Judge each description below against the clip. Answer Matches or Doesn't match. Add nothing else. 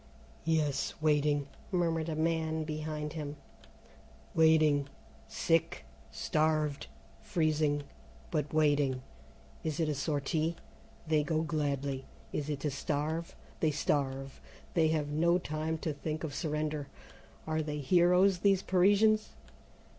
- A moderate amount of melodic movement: Doesn't match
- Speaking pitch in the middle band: Matches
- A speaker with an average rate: Doesn't match